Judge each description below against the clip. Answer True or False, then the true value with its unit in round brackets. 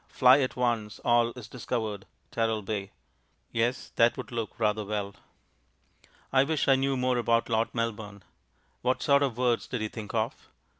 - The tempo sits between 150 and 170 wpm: True (160 wpm)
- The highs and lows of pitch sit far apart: False (2.6 semitones)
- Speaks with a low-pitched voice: True (115 Hz)